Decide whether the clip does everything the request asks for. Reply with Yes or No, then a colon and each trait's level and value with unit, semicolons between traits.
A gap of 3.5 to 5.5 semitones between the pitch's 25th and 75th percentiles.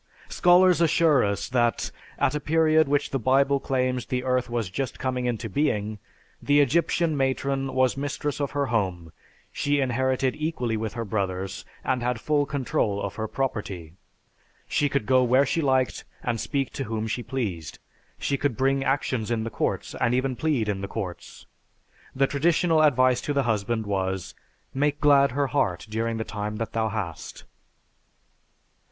Yes: average, 4.2 semitones